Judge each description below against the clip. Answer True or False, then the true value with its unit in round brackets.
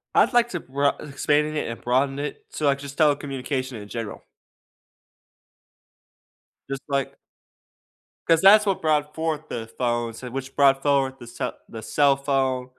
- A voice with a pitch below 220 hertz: True (140 Hz)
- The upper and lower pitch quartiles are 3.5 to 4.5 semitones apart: False (2.5 semitones)